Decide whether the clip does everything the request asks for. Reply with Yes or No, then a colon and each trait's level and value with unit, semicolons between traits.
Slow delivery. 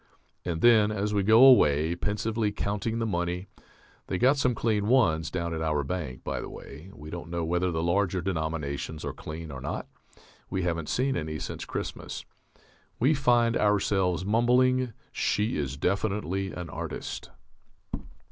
No: average, 160 wpm